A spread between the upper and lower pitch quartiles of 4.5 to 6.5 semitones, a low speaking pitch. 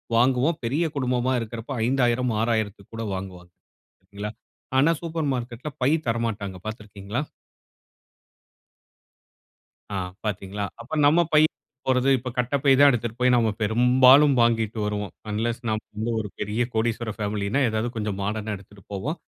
No: average, 3.2 semitones; low, 115 Hz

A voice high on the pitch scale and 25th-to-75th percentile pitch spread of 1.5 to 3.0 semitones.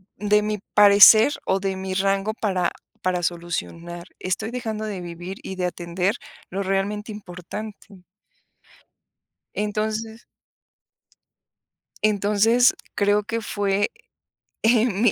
Yes: high, 205 Hz; narrow, 2.5 semitones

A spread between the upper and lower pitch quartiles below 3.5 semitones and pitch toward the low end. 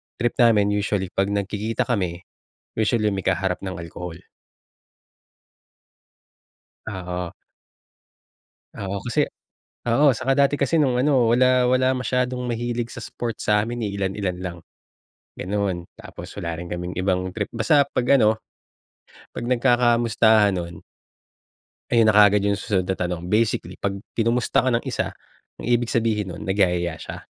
No: average, 4.2 semitones; low, 105 Hz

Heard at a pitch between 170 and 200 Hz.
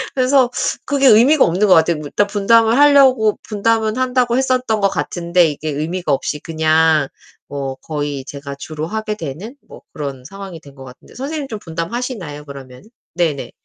Yes: medium, 185 Hz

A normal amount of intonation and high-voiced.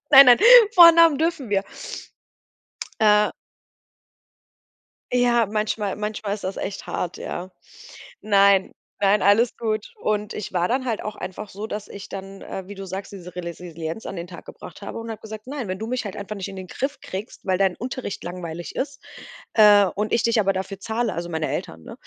Yes: average, 3.0 semitones; high, 205 Hz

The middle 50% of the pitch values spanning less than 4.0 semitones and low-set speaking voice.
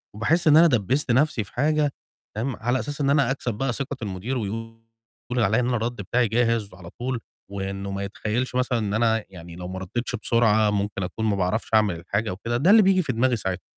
No: average, 4.3 semitones; low, 115 Hz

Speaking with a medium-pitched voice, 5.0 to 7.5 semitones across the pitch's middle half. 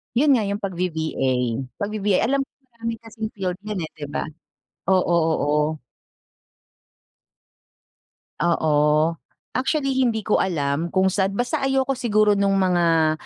No: high, 195 Hz; average, 5.3 semitones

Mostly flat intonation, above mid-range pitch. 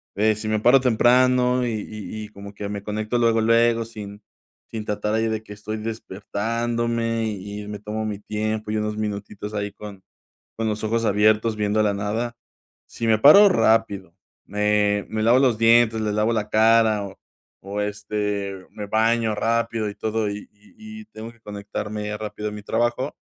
No: narrow, 1.7 semitones; low, 110 Hz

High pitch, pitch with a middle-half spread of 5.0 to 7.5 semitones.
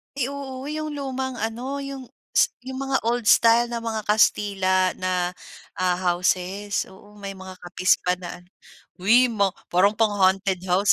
Yes: high, 210 Hz; wide, 5.5 semitones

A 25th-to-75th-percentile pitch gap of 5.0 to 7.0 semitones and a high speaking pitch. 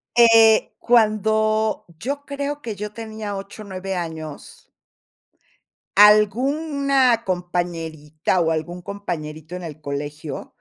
Yes: wide, 5.4 semitones; high, 200 Hz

